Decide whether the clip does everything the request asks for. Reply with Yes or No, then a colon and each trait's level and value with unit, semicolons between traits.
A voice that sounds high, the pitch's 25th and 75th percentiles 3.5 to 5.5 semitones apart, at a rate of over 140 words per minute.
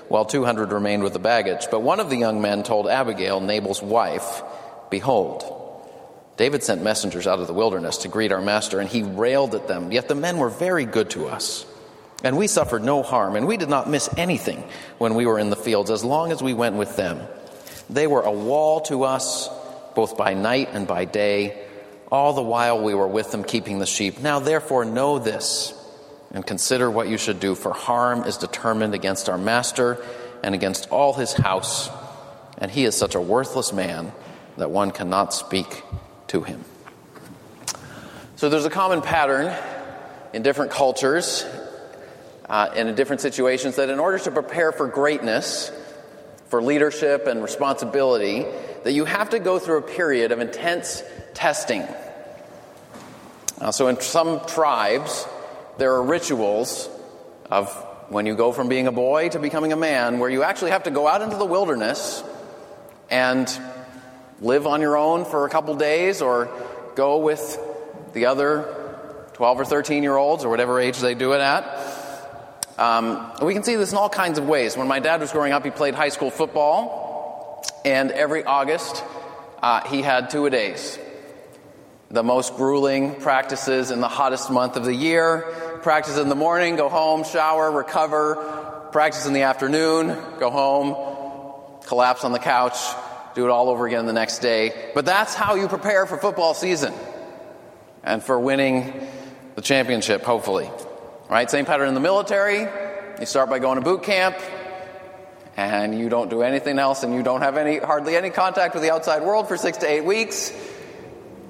No: low, 135 Hz; average, 4.3 semitones; average, 180 wpm